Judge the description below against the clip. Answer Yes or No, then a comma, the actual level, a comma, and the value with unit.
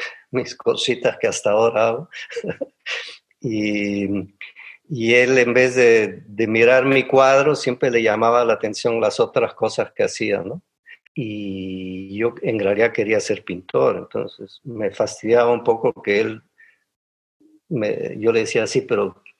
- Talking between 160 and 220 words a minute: No, average, 145 wpm